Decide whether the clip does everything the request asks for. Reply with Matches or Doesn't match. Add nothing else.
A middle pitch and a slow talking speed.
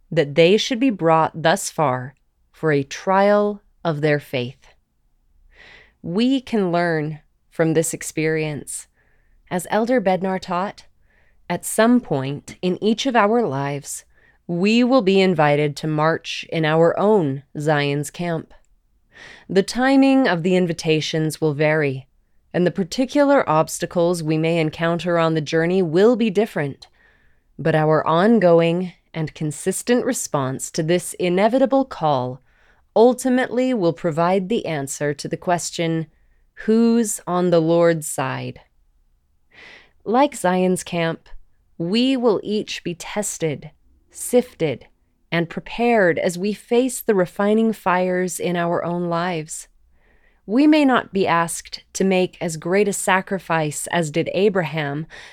Matches